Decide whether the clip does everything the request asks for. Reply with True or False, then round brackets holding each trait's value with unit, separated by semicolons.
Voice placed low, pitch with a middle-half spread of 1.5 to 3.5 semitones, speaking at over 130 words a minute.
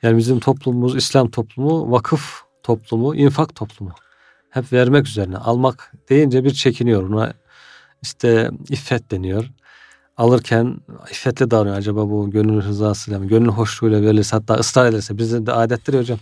True (115 Hz; 3.2 semitones; 140 wpm)